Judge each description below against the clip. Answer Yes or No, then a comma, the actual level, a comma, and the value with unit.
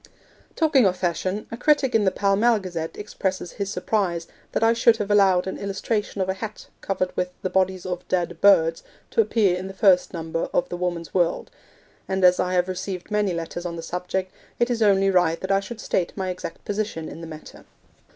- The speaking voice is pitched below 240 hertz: Yes, high, 190 Hz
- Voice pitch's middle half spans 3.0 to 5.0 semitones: No, narrow, 2.5 semitones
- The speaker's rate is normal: No, fast, 210 wpm